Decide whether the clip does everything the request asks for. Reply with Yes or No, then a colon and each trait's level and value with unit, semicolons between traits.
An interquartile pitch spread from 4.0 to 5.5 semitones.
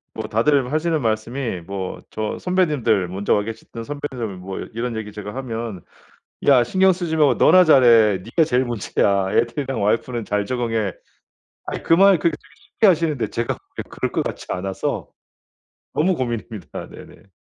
No: wide, 5.9 semitones